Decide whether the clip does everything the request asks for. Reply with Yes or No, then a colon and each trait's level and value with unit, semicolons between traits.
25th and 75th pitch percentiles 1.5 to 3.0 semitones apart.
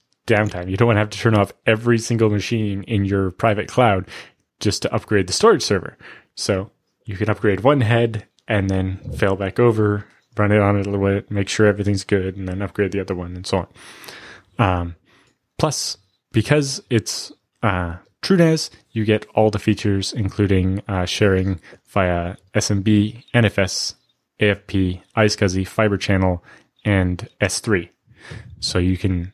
Yes: narrow, 2.6 semitones